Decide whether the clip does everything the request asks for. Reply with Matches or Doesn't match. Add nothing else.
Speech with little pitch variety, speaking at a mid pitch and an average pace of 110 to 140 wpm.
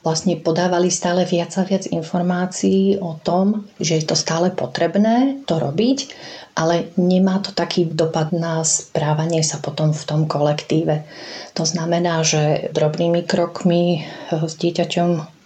Matches